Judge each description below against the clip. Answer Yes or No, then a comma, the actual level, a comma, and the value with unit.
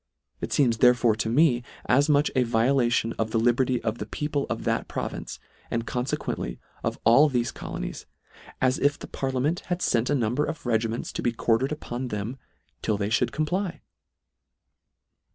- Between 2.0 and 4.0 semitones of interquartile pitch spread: Yes, average, 3.6 semitones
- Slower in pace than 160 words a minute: No, average, 170 wpm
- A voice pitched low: Yes, low, 125 Hz